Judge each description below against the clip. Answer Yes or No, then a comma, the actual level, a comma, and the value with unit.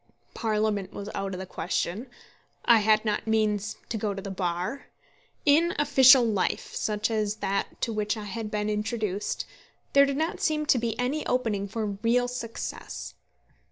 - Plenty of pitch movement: No, average, 3.2 semitones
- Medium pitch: No, high, 215 Hz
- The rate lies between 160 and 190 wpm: Yes, average, 165 wpm